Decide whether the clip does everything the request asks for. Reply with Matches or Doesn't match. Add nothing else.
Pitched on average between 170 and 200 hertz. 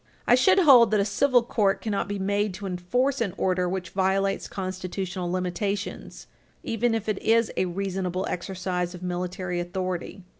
Matches